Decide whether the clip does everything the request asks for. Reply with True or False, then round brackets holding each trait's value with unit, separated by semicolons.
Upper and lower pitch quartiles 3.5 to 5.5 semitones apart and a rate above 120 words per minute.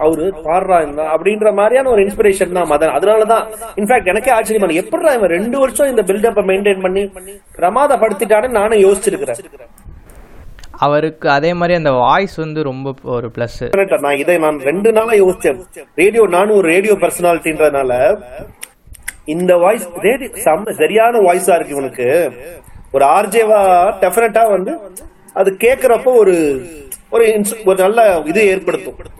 True (5.1 semitones; 130 wpm)